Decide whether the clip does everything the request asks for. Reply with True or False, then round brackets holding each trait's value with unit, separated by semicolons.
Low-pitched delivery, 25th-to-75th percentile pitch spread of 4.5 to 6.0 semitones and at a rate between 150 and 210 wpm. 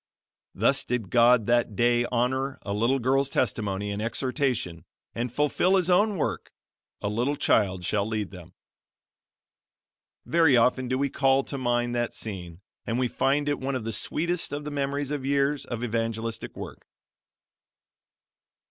False (125 Hz; 3.7 semitones; 155 wpm)